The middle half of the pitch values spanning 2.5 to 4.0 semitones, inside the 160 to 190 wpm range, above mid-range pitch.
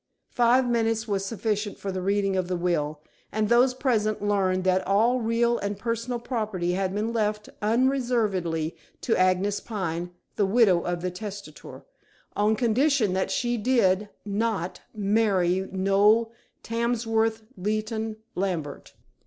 No: average, 3.4 semitones; slow, 135 wpm; high, 210 Hz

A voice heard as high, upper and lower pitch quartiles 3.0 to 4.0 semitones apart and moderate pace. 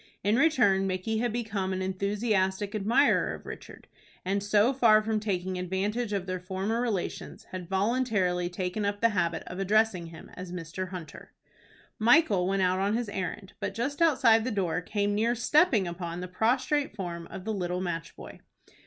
Yes: high, 200 Hz; average, 3.4 semitones; average, 175 wpm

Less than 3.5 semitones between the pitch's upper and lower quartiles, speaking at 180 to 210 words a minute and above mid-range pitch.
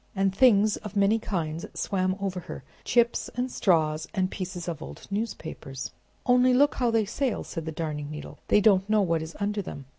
No: average, 4.7 semitones; average, 190 wpm; high, 195 Hz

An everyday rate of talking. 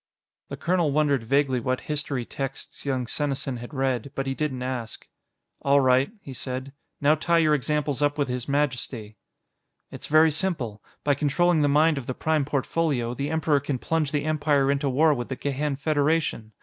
Yes: average, 180 wpm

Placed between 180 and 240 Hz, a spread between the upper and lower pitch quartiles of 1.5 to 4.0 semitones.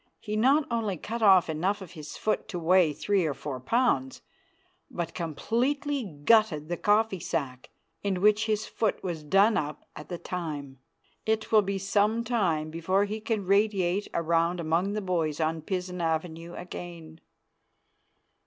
No: medium, 185 Hz; average, 4.6 semitones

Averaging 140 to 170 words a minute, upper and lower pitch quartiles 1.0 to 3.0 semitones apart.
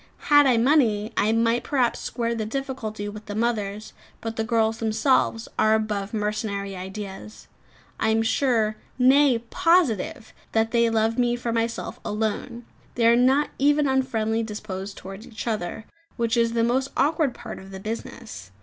Yes: average, 160 wpm; narrow, 2.4 semitones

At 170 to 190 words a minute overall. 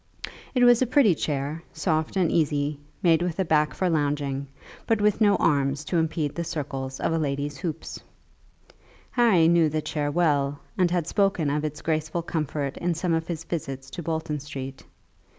Yes: average, 180 wpm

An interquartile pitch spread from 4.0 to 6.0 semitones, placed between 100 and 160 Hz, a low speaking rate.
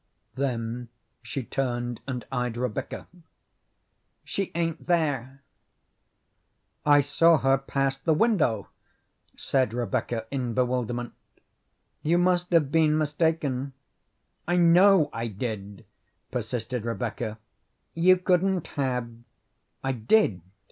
Yes: average, 5.2 semitones; low, 135 Hz; slow, 100 wpm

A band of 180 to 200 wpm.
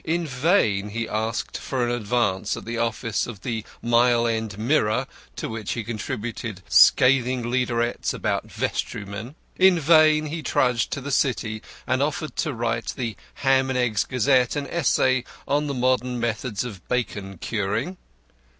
No: average, 155 wpm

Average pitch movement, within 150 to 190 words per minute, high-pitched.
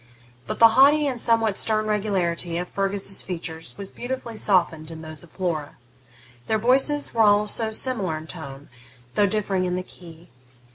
Yes: average, 4.7 semitones; average, 160 wpm; high, 195 Hz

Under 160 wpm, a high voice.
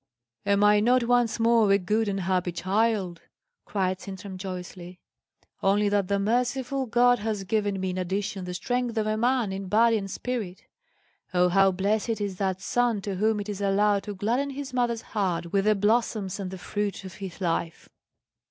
No: average, 185 wpm; high, 205 Hz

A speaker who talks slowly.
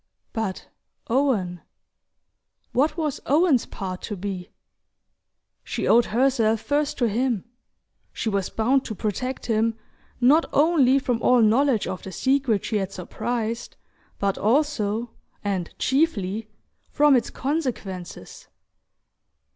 Yes: slow, 115 wpm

